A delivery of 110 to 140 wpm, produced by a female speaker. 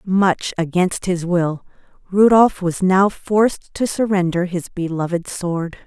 Yes: slow, 135 wpm; female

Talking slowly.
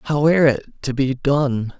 No: average, 200 wpm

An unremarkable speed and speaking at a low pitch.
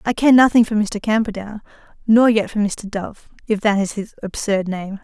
No: average, 190 wpm; high, 210 Hz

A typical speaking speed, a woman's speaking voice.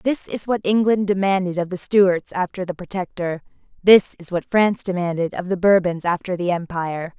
Yes: average, 185 wpm; female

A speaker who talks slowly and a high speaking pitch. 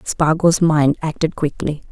No: slow, 125 wpm; medium, 155 Hz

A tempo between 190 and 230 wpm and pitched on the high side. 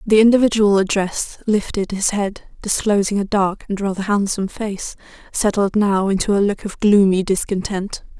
No: average, 155 wpm; high, 200 Hz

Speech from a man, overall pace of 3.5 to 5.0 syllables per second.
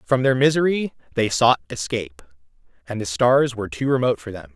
No: male; 6.0 syllables/s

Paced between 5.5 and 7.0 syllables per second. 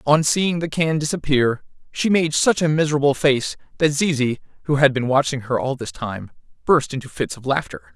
No: 5.2 syllables/s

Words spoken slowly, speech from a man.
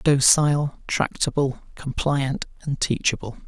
Yes: slow, 85 wpm; male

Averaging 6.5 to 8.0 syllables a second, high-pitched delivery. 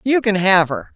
No: 4.7 syllables/s; high, 205 Hz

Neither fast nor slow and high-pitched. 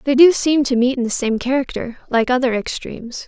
No: fast, 220 wpm; very high, 255 Hz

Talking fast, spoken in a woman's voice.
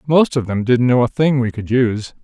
No: fast, 270 wpm; male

